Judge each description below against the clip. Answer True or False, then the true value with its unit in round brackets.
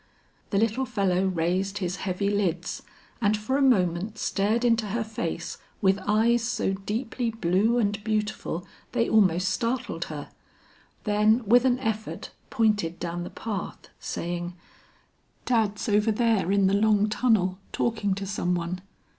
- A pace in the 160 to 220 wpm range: False (145 wpm)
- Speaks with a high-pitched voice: True (205 Hz)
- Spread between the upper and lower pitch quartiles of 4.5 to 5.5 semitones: False (3.3 semitones)